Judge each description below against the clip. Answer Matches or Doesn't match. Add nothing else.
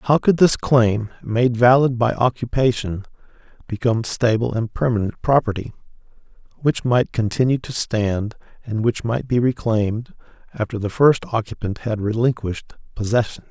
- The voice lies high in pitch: Doesn't match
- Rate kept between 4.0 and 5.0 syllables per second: Matches